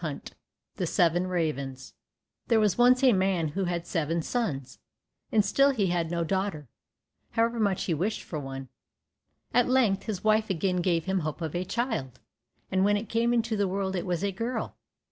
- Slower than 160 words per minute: No, average, 185 wpm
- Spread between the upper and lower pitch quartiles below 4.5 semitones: No, average, 4.8 semitones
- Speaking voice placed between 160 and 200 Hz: Yes, high, 190 Hz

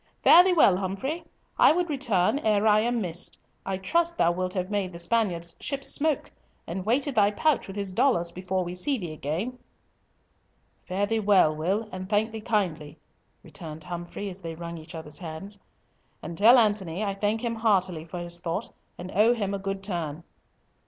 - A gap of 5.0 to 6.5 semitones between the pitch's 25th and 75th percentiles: No, average, 4.3 semitones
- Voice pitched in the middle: No, high, 195 Hz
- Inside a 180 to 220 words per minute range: Yes, average, 190 wpm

